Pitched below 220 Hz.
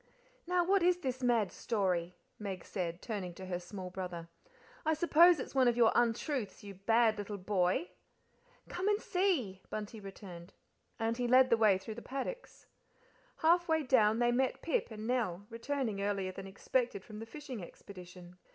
No: high, 225 Hz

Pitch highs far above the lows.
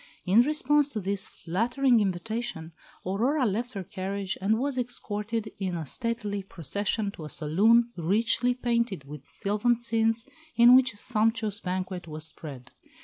No: average, 4.2 semitones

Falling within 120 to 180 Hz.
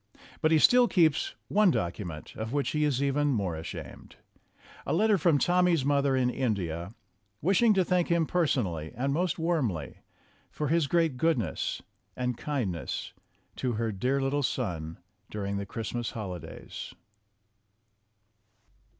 Yes: low, 135 Hz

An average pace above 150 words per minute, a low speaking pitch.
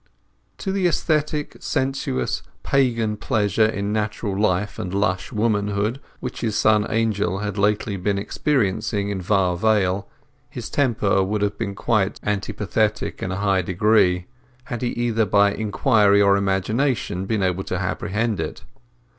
No: average, 140 wpm; low, 105 Hz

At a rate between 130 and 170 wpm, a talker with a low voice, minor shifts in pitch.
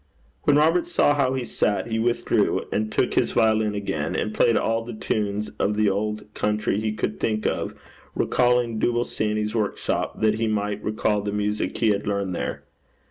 No: average, 185 wpm; low, 110 Hz; narrow, 1.5 semitones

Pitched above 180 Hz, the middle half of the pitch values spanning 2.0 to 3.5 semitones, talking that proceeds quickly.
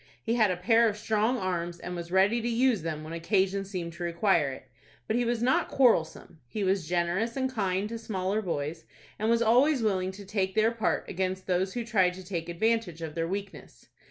No: high, 190 Hz; average, 4.5 semitones; fast, 215 wpm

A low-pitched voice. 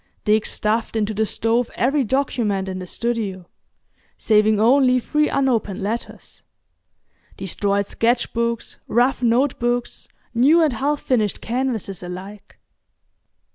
No: high, 230 Hz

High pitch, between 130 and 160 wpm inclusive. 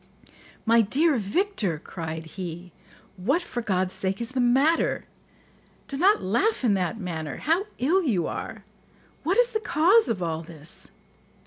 Yes: high, 225 Hz; average, 150 wpm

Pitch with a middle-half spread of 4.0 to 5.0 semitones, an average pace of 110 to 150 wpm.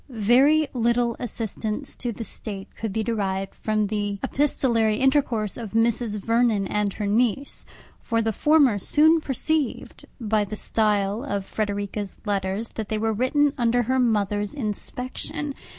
No: average, 3.3 semitones; average, 145 wpm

